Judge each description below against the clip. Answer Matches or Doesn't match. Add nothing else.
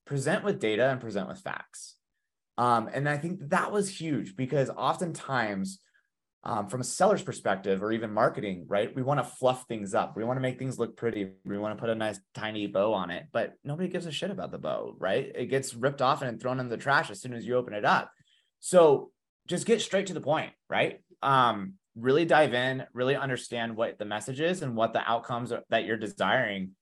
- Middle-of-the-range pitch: Doesn't match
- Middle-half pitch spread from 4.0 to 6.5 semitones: Matches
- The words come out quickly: Matches